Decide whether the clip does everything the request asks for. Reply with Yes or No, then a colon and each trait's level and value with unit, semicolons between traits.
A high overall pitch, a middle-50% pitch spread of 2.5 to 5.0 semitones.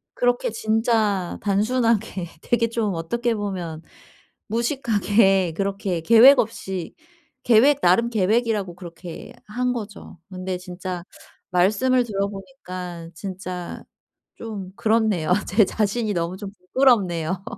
Yes: high, 200 Hz; average, 4.0 semitones